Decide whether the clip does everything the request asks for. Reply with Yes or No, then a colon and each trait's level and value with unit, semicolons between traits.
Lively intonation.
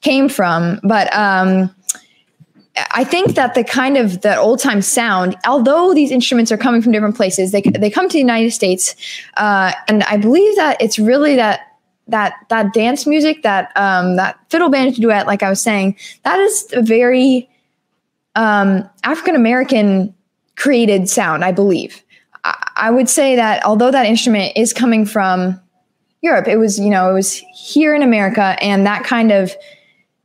No: average, 4.7 semitones